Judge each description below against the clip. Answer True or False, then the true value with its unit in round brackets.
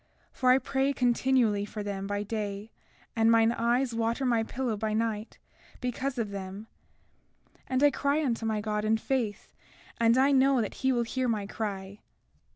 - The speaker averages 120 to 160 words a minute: False (170 wpm)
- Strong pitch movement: False (3.5 semitones)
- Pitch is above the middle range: True (230 Hz)